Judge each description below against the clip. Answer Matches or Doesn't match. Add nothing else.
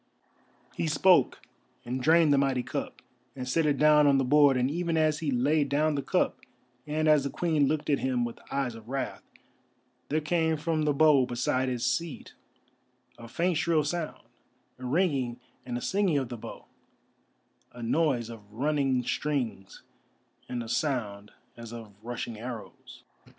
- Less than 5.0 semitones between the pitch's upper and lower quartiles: Matches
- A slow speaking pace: Doesn't match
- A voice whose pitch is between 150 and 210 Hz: Doesn't match